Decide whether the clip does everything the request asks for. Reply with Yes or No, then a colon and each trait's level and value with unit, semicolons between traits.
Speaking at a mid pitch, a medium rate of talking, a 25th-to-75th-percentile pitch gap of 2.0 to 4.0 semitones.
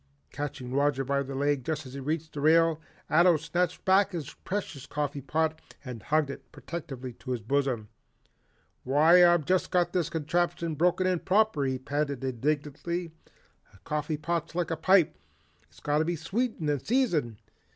Yes: medium, 155 Hz; average, 170 wpm; average, 3.6 semitones